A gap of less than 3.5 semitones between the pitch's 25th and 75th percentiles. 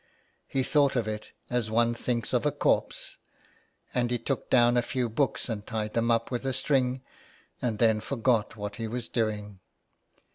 Yes: narrow, 2.4 semitones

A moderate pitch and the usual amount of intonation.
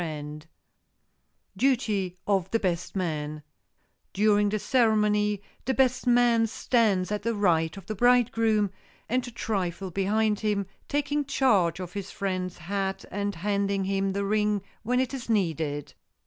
No: high, 205 Hz; average, 3.5 semitones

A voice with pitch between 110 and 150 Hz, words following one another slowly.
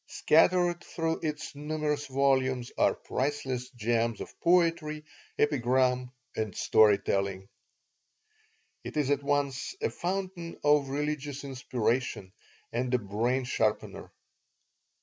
Yes: low, 135 Hz; slow, 110 wpm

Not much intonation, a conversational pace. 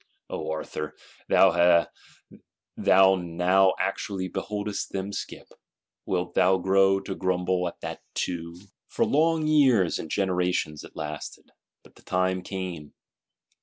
No: narrow, 1.8 semitones; slow, 115 wpm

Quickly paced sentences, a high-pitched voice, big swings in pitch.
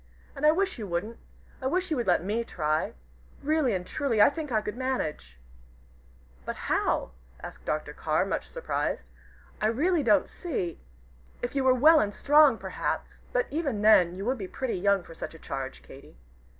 No: average, 185 wpm; high, 230 Hz; wide, 7.8 semitones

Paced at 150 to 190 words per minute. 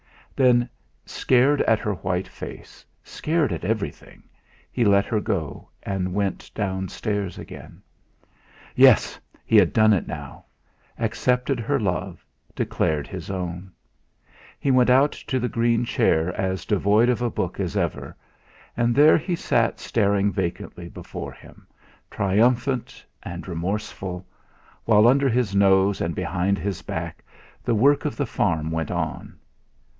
No: average, 140 wpm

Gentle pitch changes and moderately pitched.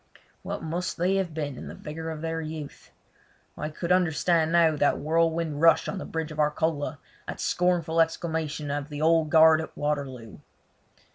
Yes: narrow, 1.7 semitones; medium, 160 Hz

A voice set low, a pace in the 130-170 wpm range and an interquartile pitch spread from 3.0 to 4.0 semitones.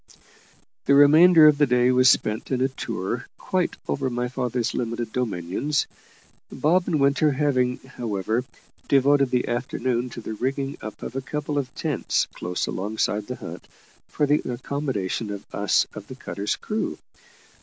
Yes: low, 130 Hz; average, 155 wpm; average, 3.5 semitones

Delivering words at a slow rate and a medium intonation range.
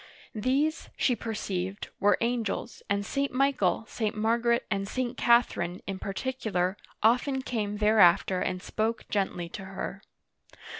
Yes: slow, 130 wpm; average, 3.7 semitones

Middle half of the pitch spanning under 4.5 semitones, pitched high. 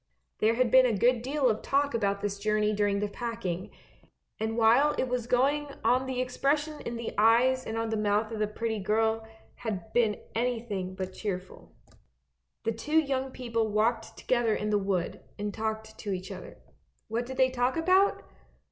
Yes: average, 3.2 semitones; high, 225 Hz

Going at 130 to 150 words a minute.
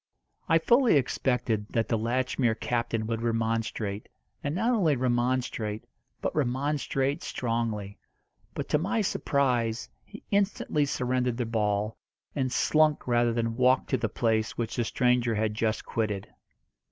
Yes: average, 140 wpm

